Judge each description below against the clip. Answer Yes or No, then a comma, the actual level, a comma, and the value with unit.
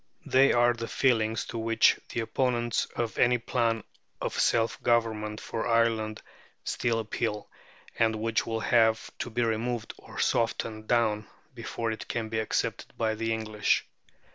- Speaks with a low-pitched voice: Yes, low, 115 Hz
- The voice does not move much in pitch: Yes, narrow, 1.2 semitones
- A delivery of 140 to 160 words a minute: Yes, average, 150 wpm